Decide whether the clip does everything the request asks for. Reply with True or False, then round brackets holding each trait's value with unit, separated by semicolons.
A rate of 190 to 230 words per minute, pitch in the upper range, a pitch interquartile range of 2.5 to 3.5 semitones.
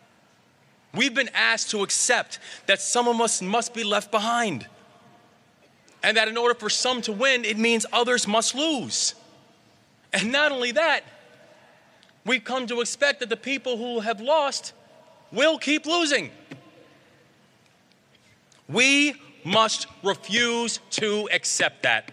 False (135 wpm; 235 Hz; 3.0 semitones)